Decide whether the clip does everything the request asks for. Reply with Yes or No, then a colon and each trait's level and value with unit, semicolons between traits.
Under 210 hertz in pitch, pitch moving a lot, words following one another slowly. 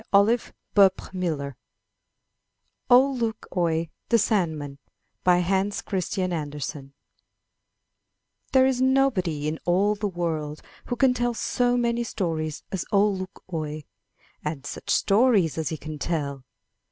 Yes: medium, 185 Hz; wide, 6.4 semitones; slow, 130 wpm